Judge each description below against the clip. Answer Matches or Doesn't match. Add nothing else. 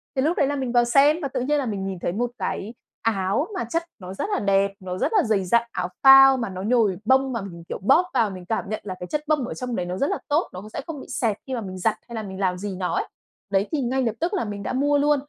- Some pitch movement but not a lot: Doesn't match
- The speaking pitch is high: Matches